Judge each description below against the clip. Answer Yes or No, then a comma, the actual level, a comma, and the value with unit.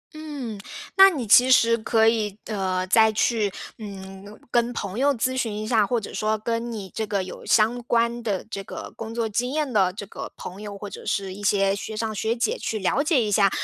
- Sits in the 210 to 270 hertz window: Yes, high, 220 Hz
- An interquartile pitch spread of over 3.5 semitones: No, average, 2.8 semitones